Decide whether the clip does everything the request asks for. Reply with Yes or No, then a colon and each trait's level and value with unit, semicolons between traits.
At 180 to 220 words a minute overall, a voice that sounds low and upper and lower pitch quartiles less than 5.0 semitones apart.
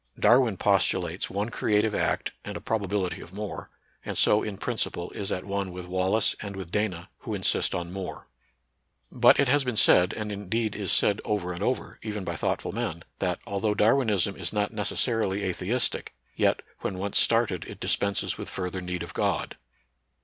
Yes: average, 185 wpm; low, 100 Hz; average, 2.8 semitones